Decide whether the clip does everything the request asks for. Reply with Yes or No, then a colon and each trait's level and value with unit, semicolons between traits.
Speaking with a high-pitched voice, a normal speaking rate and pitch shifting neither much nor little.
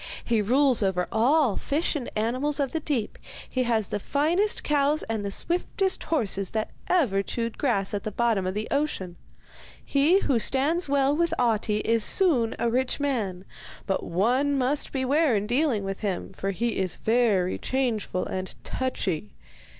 No: high, 240 Hz; average, 165 wpm; wide, 5.7 semitones